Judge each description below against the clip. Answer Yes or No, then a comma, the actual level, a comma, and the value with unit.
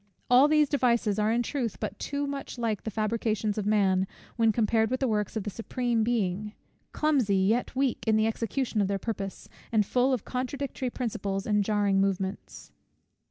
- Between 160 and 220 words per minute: Yes, average, 180 wpm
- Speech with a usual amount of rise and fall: Yes, average, 3.4 semitones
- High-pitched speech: Yes, high, 220 Hz